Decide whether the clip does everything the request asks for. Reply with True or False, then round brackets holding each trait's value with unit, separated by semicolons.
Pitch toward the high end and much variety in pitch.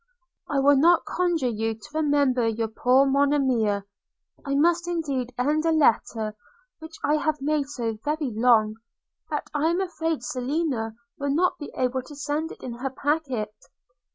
False (280 Hz; 4.2 semitones)